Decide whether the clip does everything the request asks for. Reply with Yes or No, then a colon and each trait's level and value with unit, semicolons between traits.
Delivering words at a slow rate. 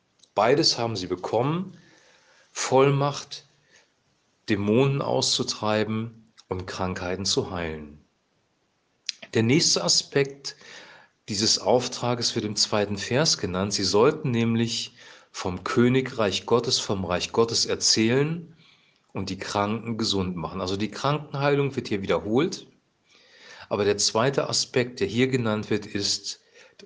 Yes: slow, 115 wpm